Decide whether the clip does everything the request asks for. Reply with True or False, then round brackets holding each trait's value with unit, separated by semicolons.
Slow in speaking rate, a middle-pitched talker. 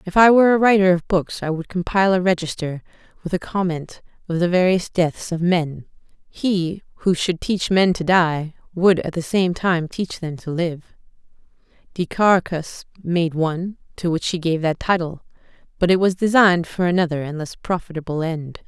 False (180 wpm; 175 Hz)